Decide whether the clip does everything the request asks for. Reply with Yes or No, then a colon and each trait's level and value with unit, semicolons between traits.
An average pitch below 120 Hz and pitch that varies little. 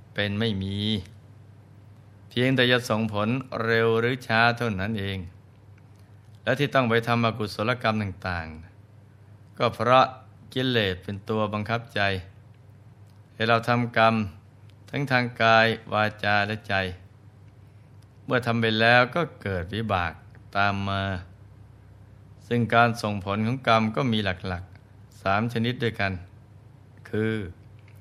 Yes: low, 110 Hz; narrow, 2.0 semitones